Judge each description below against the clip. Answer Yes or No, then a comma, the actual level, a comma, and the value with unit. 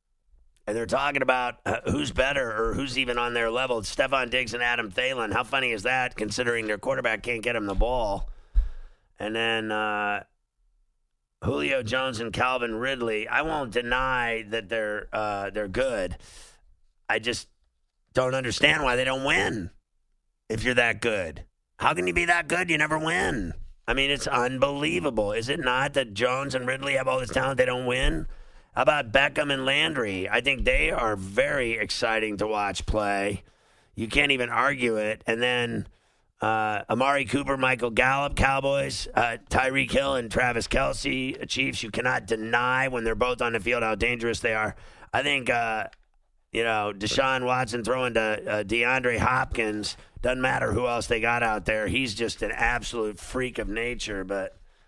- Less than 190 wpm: Yes, average, 175 wpm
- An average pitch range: Yes, average, 3.3 semitones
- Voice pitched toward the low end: Yes, low, 120 Hz